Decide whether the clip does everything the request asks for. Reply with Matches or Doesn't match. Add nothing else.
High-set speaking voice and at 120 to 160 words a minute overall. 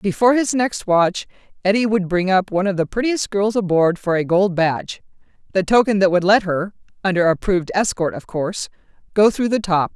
Doesn't match